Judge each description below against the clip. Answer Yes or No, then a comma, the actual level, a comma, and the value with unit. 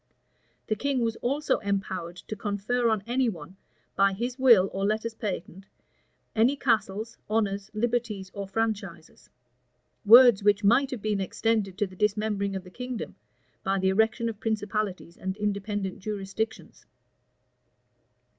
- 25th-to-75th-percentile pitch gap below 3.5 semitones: Yes, average, 2.7 semitones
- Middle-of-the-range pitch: No, high, 210 Hz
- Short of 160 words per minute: Yes, slow, 135 wpm